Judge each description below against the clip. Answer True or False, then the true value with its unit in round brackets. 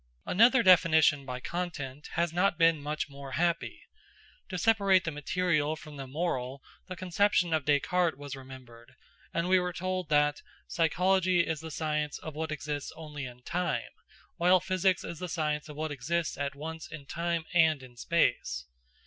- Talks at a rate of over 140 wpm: True (165 wpm)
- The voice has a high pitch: False (160 Hz)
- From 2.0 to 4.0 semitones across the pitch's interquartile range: True (3.5 semitones)